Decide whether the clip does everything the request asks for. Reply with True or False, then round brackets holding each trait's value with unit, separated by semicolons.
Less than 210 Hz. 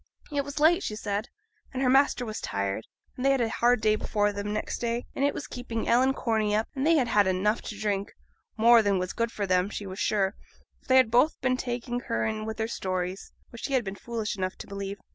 False (220 Hz)